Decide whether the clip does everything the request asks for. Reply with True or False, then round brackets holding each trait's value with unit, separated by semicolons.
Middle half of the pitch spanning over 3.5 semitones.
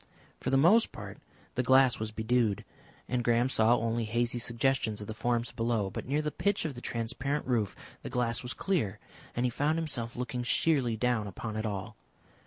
False (2.8 semitones)